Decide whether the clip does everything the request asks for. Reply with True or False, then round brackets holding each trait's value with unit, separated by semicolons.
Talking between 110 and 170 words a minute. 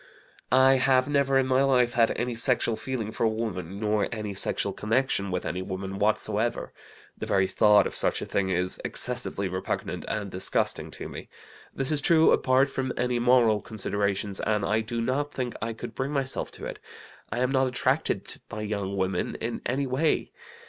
False (185 wpm)